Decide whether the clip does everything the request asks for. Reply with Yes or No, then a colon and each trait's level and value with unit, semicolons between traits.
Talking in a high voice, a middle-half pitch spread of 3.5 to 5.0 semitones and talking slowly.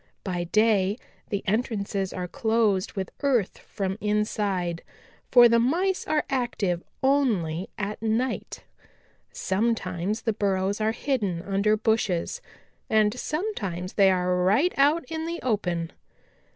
Yes: high, 210 Hz; average, 4.3 semitones; slow, 125 wpm